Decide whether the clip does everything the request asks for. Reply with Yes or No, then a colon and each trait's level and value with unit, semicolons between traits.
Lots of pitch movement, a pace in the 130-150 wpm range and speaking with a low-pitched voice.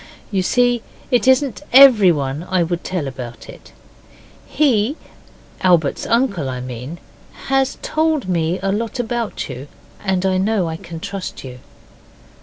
No: wide, 6.9 semitones; average, 140 wpm; high, 190 Hz